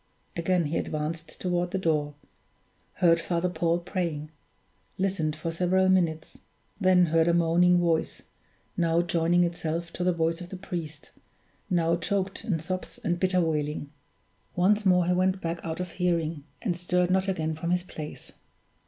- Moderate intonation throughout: No, narrow, 1.8 semitones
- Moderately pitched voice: Yes, medium, 170 Hz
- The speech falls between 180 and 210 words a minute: No, average, 160 wpm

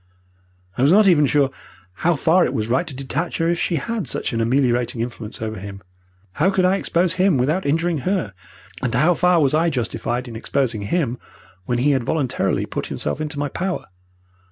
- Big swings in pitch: Yes, wide, 6.1 semitones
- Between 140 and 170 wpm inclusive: No, average, 200 wpm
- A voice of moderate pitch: Yes, medium, 145 Hz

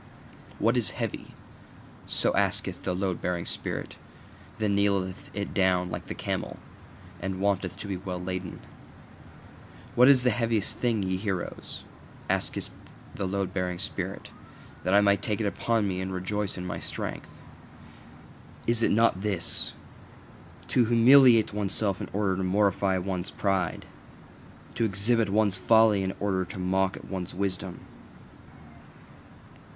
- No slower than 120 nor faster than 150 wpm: Yes, average, 140 wpm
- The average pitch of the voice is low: Yes, low, 100 Hz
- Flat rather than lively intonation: Yes, narrow, 2.2 semitones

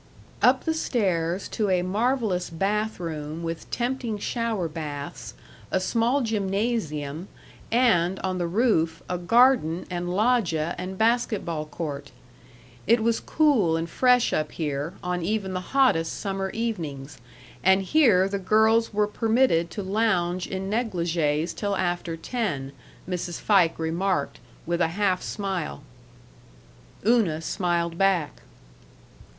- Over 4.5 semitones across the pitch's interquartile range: Yes, average, 4.9 semitones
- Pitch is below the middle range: No, medium, 185 Hz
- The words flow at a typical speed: No, slow, 125 wpm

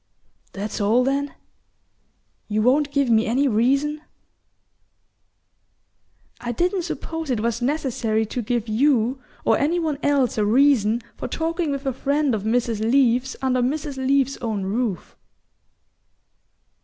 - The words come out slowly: Yes, slow, 130 wpm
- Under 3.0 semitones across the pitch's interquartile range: No, average, 4.0 semitones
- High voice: Yes, very high, 255 Hz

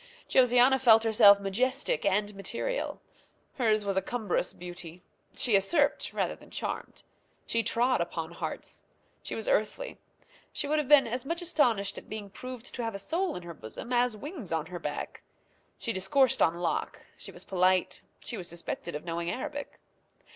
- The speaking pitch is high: Yes, high, 220 Hz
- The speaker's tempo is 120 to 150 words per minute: No, average, 170 wpm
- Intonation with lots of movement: Yes, wide, 6.0 semitones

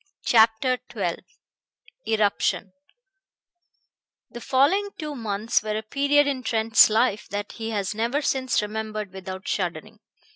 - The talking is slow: Yes, slow, 120 wpm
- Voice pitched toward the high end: Yes, high, 220 Hz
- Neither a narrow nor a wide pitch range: Yes, average, 3.6 semitones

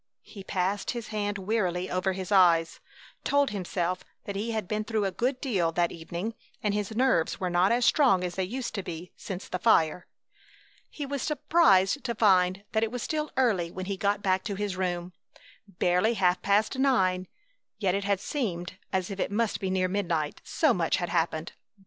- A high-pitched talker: Yes, high, 195 Hz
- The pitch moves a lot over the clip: No, average, 3.6 semitones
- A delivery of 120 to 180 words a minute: No, average, 195 wpm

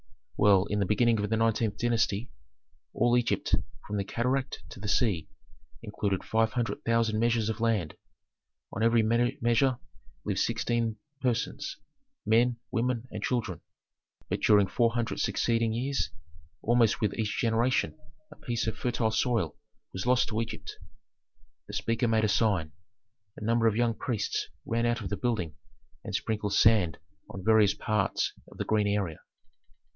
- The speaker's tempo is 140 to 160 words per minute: Yes, average, 155 wpm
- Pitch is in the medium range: No, low, 115 Hz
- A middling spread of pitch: No, narrow, 2.3 semitones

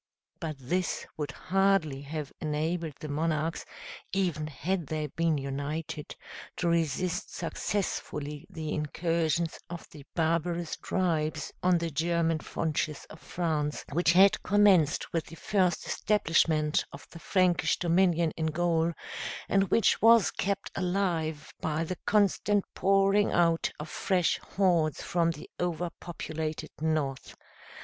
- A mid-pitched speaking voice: Yes, medium, 165 Hz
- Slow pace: Yes, slow, 125 wpm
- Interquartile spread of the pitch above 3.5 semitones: No, average, 2.7 semitones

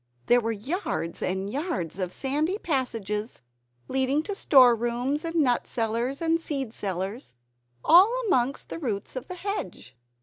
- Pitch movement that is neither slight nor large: No, wide, 6.3 semitones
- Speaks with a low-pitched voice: No, very high, 255 Hz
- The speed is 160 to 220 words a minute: No, average, 145 wpm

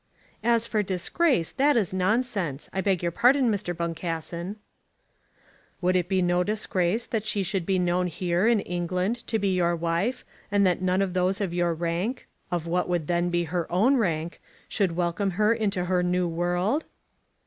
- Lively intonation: No, average, 3.2 semitones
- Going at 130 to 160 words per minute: No, average, 180 wpm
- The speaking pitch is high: No, medium, 180 Hz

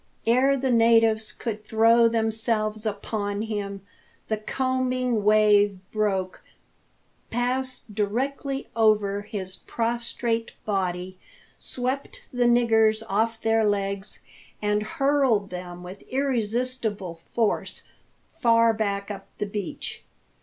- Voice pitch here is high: Yes, high, 220 Hz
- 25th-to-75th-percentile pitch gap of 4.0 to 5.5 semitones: No, average, 2.7 semitones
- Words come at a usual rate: No, slow, 100 wpm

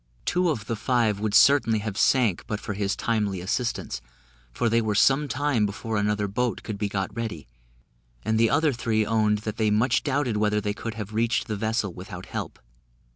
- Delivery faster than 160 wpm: Yes, average, 195 wpm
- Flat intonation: Yes, narrow, 2.2 semitones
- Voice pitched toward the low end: Yes, low, 110 Hz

